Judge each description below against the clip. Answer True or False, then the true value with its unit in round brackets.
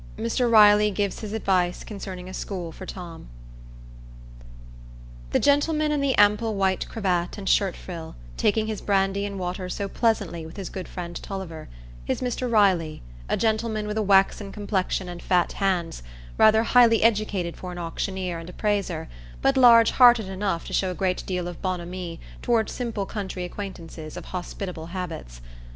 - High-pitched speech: True (195 Hz)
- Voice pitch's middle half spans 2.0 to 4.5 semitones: True (3.2 semitones)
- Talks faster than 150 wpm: True (165 wpm)